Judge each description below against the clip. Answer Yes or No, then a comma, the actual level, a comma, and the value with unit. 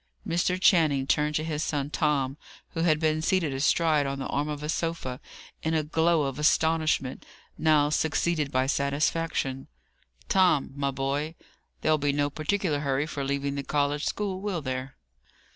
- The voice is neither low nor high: Yes, medium, 150 Hz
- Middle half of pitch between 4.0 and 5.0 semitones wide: No, narrow, 2.5 semitones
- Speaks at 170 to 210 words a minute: No, average, 160 wpm